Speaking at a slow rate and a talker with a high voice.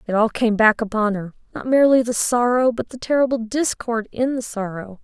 No: fast, 205 wpm; high, 230 Hz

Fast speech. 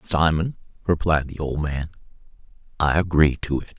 No: average, 145 wpm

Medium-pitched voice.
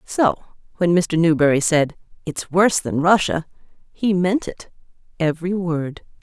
Yes: medium, 170 Hz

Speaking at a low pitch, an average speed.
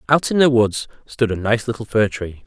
No: low, 115 Hz; fast, 245 wpm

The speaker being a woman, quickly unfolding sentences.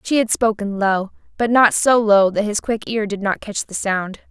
Yes: female; fast, 235 wpm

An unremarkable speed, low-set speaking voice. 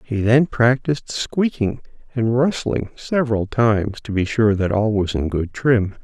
Yes: average, 170 wpm; low, 115 Hz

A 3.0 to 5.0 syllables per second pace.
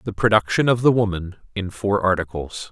Yes: 4.5 syllables/s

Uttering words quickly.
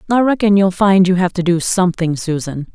Yes: fast, 220 wpm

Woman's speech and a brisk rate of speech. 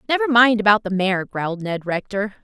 No: female; average, 195 wpm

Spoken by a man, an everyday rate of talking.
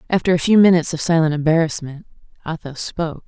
No: female; average, 165 wpm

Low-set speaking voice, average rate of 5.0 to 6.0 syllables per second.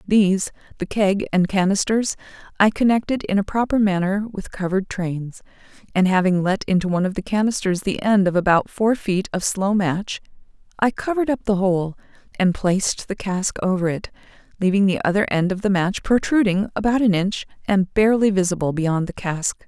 No: high, 195 Hz; 5.3 syllables/s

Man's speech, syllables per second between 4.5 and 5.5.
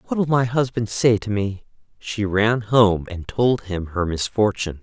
No: male; 4.3 syllables/s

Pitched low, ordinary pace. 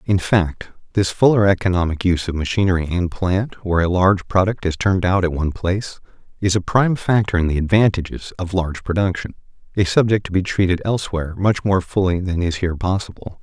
Yes: very low, 90 Hz; average, 190 wpm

